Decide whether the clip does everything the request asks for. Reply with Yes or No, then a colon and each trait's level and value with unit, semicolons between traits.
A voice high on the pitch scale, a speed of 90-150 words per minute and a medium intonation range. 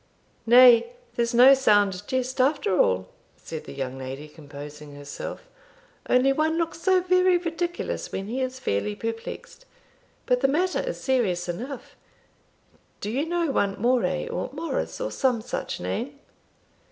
No: very high, 250 Hz; average, 145 wpm; wide, 8.3 semitones